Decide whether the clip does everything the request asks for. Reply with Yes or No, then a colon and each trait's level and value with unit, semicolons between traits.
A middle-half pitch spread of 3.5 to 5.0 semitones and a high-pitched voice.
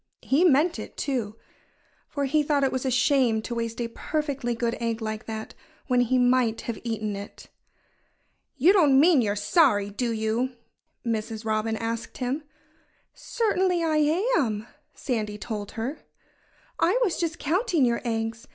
Yes: average, 4.3 semitones; high, 240 Hz